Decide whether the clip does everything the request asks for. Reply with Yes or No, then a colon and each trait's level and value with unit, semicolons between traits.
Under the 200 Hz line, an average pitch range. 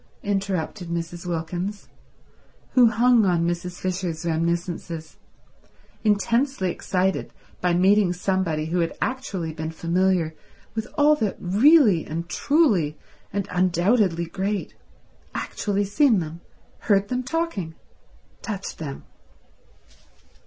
Yes: medium, 185 Hz; average, 3.7 semitones